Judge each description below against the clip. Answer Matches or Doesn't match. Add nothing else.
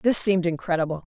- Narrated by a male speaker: Doesn't match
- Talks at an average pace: Matches